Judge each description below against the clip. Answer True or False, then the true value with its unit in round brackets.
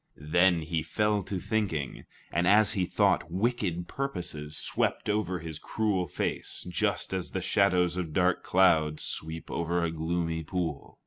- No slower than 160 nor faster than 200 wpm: False (150 wpm)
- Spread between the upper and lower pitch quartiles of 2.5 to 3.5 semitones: True (3.0 semitones)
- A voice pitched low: True (90 Hz)